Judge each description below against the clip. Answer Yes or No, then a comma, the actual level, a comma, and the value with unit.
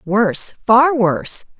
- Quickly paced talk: No, slow, 115 wpm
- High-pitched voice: Yes, high, 215 Hz